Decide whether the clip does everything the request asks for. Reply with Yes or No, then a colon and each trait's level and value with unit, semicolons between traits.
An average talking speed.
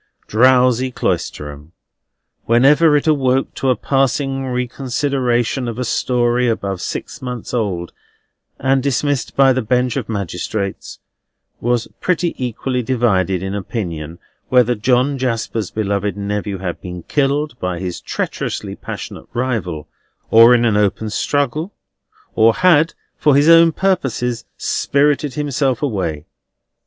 No: slow, 125 wpm